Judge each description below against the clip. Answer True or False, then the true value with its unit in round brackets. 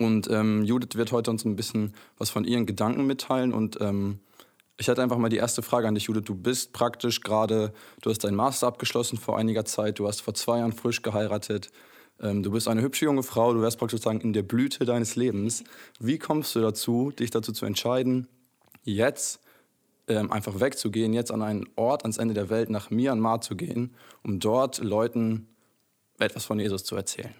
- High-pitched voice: False (115 Hz)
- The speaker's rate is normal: False (200 wpm)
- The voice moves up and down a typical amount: False (2.0 semitones)